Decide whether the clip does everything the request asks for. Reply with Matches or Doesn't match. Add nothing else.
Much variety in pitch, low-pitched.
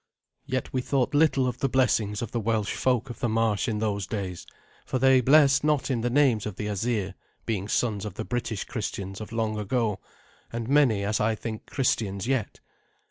Doesn't match